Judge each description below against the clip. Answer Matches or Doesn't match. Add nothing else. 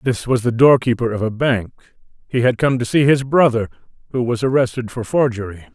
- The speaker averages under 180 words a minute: Doesn't match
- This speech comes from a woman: Doesn't match